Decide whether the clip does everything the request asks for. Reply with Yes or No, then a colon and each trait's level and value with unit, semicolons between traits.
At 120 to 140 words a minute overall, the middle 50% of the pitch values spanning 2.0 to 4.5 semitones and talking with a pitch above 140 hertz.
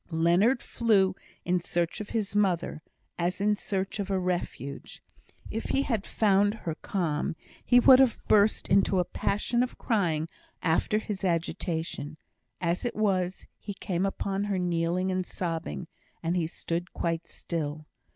No: average, 150 wpm; average, 3.4 semitones; medium, 185 Hz